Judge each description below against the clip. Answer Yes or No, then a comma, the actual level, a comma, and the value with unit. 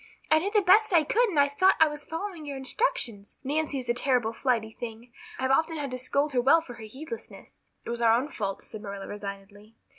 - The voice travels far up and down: Yes, wide, 5.7 semitones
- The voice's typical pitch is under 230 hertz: No, very high, 265 Hz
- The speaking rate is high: Yes, fast, 230 wpm